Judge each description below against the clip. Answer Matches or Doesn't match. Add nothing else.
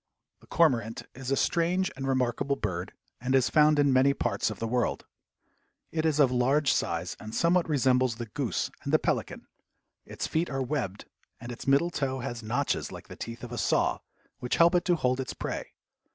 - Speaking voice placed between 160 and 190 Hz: Doesn't match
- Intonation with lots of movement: Doesn't match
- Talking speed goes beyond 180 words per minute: Matches